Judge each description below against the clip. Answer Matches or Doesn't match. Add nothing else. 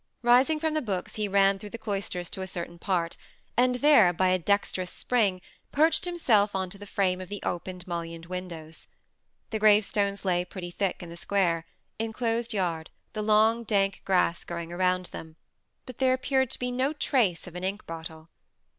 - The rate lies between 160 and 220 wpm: Matches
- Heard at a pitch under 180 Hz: Doesn't match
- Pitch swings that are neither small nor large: Matches